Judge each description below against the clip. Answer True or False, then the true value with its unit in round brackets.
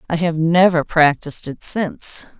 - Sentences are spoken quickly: False (150 wpm)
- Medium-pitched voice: True (165 Hz)